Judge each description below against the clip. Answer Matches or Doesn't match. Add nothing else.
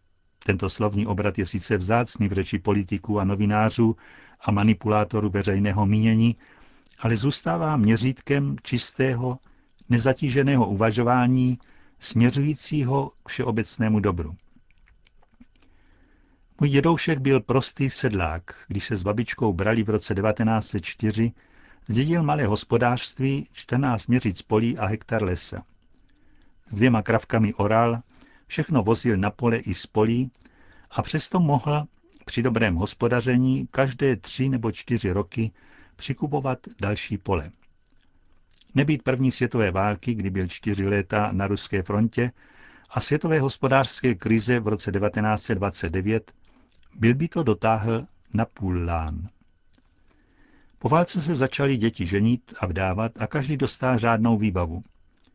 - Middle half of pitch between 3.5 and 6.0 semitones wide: Matches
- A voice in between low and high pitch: Doesn't match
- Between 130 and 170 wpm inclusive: Doesn't match